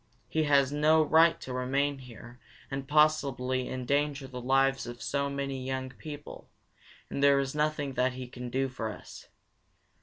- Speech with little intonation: Yes, narrow, 2.2 semitones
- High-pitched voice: No, low, 135 Hz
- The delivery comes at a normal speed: Yes, average, 160 wpm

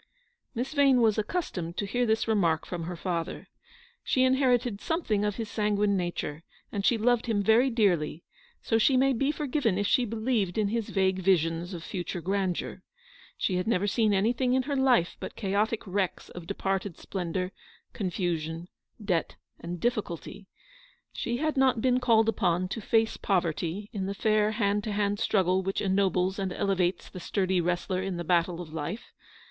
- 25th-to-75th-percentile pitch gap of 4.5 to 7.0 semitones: No, average, 4.1 semitones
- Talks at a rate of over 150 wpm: Yes, average, 175 wpm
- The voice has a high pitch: Yes, high, 200 Hz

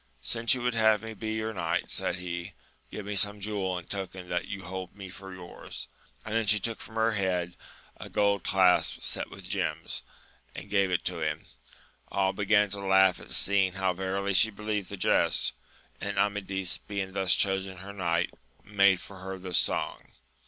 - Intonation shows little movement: Yes, narrow, 1.8 semitones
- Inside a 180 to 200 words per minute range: Yes, average, 185 wpm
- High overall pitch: No, very low, 95 Hz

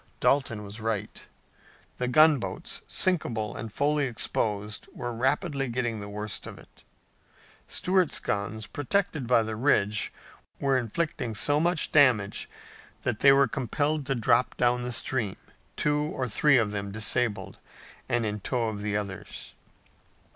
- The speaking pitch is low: Yes, low, 120 Hz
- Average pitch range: Yes, average, 4.7 semitones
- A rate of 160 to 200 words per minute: No, average, 140 wpm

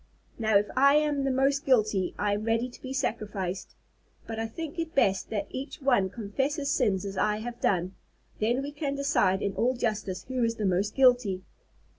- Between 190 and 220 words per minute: Yes, average, 200 wpm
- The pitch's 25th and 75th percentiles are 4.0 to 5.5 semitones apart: Yes, average, 5.0 semitones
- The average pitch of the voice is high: Yes, high, 230 Hz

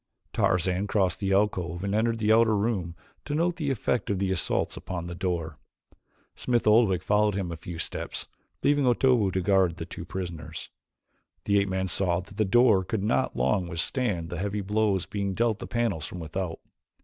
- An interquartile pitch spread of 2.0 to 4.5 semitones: Yes, average, 3.6 semitones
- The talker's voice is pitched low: Yes, low, 100 Hz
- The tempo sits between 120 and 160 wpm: No, average, 185 wpm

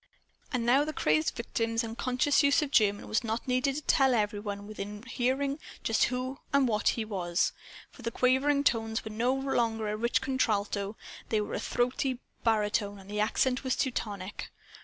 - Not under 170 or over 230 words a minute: Yes, average, 180 wpm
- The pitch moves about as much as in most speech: Yes, average, 3.7 semitones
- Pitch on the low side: No, high, 230 Hz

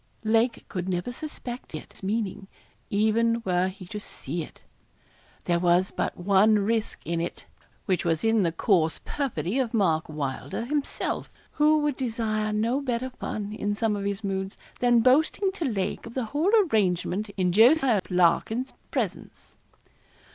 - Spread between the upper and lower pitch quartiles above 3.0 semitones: Yes, average, 4.6 semitones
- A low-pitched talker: No, high, 215 Hz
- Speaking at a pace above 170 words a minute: No, average, 155 wpm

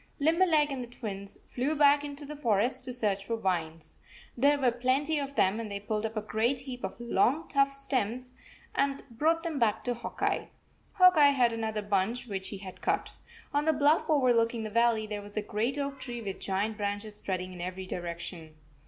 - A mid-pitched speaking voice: No, high, 235 Hz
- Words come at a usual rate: No, fast, 210 wpm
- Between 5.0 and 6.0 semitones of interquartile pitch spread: Yes, wide, 5.4 semitones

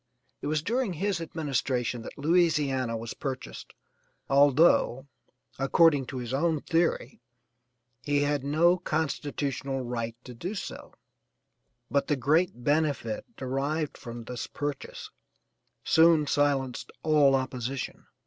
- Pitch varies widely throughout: No, average, 3.4 semitones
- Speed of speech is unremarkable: No, slow, 115 wpm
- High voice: No, medium, 140 Hz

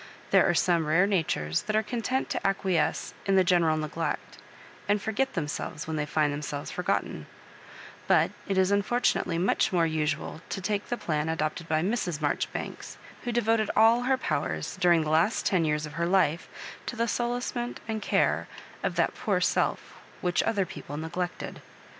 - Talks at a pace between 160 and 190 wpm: Yes, average, 175 wpm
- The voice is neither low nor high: Yes, medium, 180 Hz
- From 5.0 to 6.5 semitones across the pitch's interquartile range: Yes, average, 5.3 semitones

